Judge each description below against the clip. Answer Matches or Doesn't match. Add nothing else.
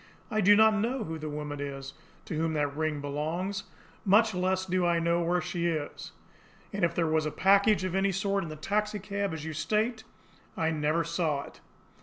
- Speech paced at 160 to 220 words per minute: Matches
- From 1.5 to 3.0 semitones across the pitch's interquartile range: Doesn't match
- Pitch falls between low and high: Matches